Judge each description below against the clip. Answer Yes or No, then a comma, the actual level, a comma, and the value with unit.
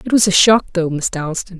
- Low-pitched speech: No, medium, 185 Hz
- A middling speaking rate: No, fast, 265 wpm